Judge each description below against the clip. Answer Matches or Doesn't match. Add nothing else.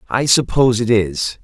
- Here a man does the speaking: Matches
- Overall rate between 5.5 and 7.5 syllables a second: Doesn't match